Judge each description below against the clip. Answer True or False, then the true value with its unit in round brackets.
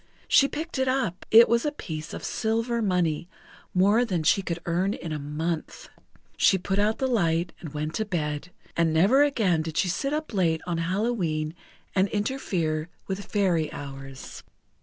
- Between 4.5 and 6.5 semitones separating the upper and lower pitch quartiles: True (5.5 semitones)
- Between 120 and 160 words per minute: False (175 wpm)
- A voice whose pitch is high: False (180 Hz)